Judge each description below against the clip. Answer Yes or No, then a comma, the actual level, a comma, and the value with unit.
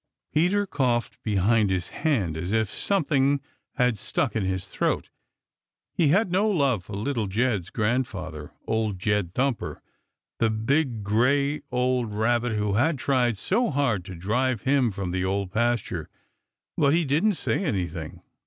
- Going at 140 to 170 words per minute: Yes, average, 150 wpm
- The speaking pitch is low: Yes, low, 115 Hz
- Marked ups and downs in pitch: Yes, wide, 5.8 semitones